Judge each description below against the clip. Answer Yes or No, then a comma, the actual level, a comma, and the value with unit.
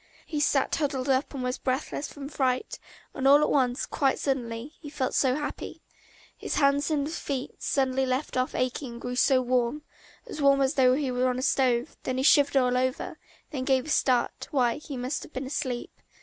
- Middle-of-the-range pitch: No, very high, 265 Hz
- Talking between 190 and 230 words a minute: Yes, fast, 205 wpm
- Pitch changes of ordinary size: No, narrow, 2.0 semitones